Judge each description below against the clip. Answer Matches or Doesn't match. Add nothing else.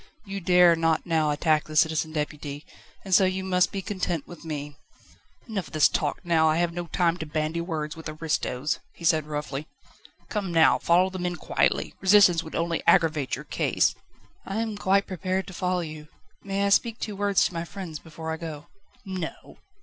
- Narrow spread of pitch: Doesn't match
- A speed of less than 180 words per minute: Doesn't match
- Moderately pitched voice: Matches